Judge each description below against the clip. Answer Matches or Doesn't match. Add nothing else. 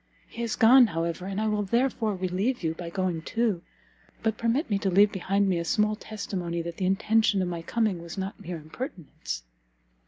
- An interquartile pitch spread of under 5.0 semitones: Matches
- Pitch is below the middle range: Doesn't match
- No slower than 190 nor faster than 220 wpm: Matches